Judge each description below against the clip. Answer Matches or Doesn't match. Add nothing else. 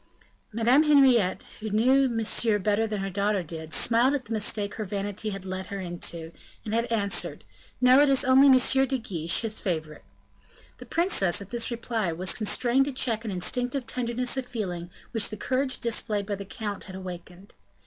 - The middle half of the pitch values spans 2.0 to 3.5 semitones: Doesn't match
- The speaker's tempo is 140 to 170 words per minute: Doesn't match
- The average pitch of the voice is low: Doesn't match